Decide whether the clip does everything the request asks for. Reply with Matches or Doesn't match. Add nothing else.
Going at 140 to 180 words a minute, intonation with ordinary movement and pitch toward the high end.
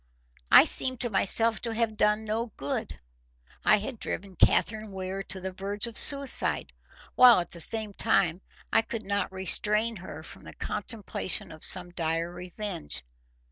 Matches